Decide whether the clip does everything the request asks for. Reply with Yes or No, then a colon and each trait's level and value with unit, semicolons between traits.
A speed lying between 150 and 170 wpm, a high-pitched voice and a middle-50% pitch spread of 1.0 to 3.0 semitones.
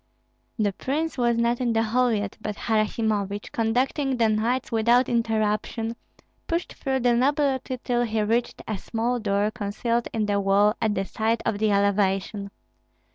Yes: average, 160 wpm; high, 225 Hz; average, 2.7 semitones